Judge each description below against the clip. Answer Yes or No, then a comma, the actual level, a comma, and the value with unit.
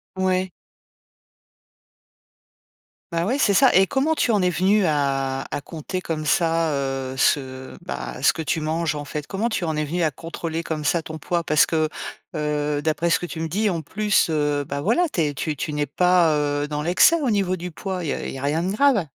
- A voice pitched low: No, medium, 160 Hz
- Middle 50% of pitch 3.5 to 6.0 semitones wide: Yes, average, 3.9 semitones